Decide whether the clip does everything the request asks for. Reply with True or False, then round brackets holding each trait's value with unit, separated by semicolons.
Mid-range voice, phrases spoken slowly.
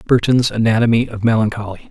False (115 Hz; 125 wpm)